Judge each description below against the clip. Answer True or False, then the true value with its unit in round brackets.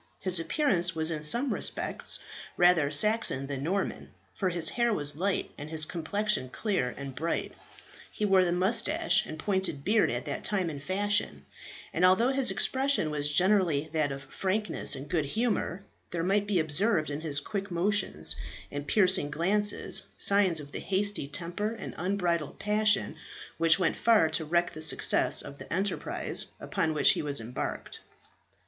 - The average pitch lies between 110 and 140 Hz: False (180 Hz)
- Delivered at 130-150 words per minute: False (165 wpm)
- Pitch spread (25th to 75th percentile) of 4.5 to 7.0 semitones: True (5.0 semitones)